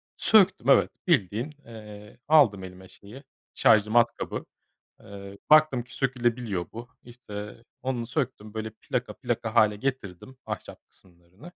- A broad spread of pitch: No, average, 4.0 semitones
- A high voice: No, low, 115 Hz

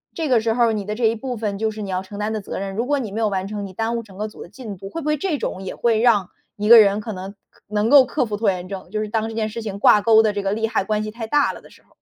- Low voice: No, high, 215 Hz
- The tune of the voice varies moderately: No, narrow, 2.3 semitones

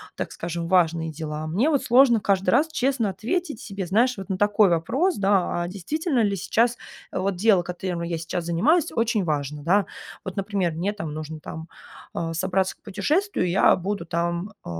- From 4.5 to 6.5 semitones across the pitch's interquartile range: Yes, average, 5.0 semitones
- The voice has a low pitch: No, high, 190 Hz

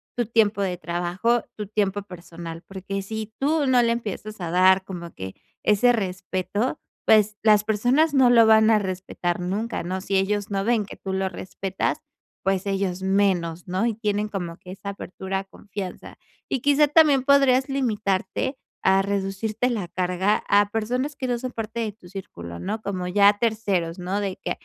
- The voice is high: Yes, high, 200 Hz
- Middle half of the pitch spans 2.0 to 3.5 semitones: Yes, average, 3.2 semitones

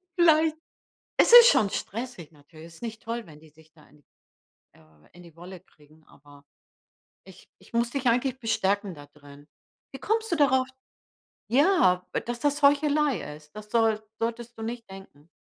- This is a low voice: No, high, 220 Hz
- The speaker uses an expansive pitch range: Yes, wide, 8.7 semitones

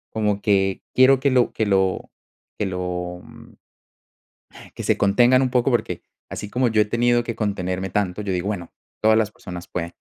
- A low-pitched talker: Yes, low, 105 Hz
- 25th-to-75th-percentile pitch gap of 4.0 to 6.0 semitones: Yes, average, 4.4 semitones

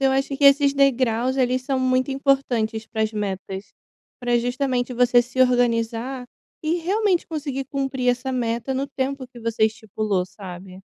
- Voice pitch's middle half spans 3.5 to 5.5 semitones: No, average, 3.1 semitones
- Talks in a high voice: Yes, very high, 250 Hz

